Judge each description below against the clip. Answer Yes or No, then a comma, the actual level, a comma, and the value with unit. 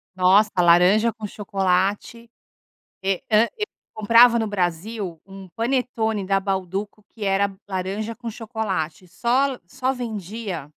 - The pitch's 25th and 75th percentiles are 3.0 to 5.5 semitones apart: Yes, average, 3.3 semitones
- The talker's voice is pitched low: No, high, 205 Hz